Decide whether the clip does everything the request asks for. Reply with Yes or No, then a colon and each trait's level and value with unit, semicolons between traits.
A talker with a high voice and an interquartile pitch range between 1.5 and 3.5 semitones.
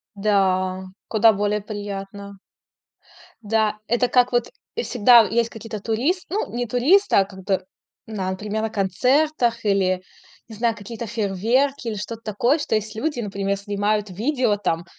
Yes: high, 215 Hz; average, 3.1 semitones